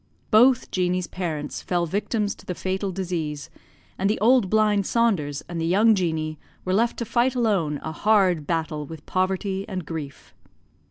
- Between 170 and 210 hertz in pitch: Yes, medium, 185 Hz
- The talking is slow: No, average, 165 wpm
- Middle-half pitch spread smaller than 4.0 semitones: No, average, 4.6 semitones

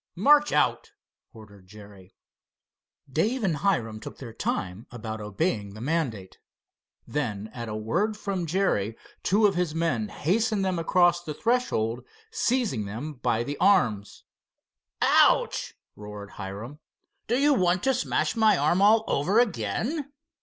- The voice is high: No, medium, 150 Hz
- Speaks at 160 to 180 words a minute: No, average, 140 wpm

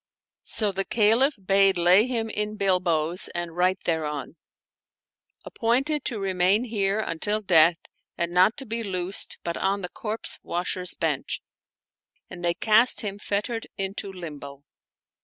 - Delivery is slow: No, average, 145 wpm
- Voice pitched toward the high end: Yes, high, 195 Hz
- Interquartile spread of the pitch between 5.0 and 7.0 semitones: No, average, 3.6 semitones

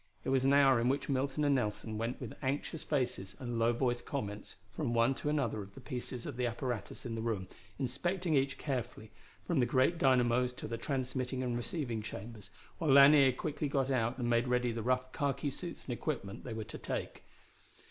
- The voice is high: No, low, 125 Hz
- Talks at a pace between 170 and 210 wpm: Yes, average, 200 wpm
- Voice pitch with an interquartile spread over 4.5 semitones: No, average, 2.9 semitones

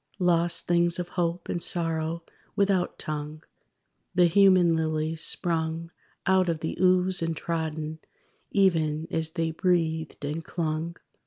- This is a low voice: No, medium, 165 Hz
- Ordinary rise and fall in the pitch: No, narrow, 1.8 semitones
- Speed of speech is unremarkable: No, slow, 130 wpm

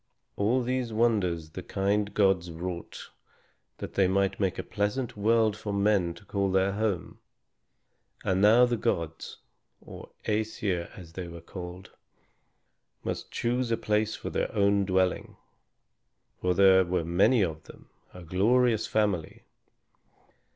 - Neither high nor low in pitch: No, low, 100 Hz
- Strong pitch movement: No, average, 3.1 semitones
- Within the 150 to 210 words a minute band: No, slow, 135 wpm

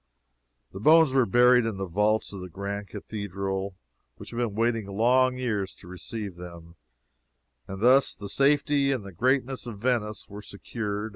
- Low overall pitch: Yes, low, 105 Hz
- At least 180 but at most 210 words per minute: No, average, 165 wpm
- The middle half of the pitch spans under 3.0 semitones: No, average, 4.1 semitones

